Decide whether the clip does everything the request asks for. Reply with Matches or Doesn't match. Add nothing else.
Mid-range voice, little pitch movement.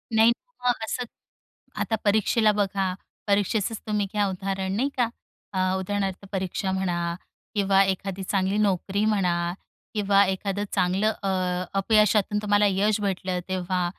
Doesn't match